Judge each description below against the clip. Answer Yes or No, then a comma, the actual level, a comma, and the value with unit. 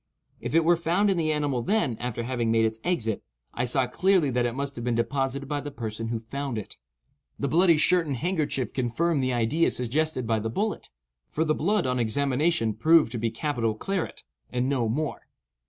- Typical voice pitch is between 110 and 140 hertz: Yes, low, 135 Hz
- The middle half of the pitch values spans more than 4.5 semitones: Yes, average, 5.2 semitones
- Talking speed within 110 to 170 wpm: No, fast, 205 wpm